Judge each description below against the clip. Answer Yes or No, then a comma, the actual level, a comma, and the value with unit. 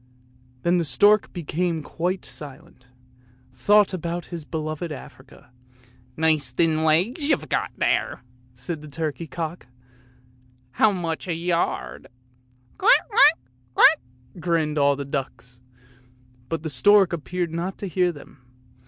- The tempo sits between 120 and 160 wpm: Yes, average, 145 wpm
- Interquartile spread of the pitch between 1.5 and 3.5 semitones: No, wide, 5.6 semitones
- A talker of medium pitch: Yes, medium, 155 Hz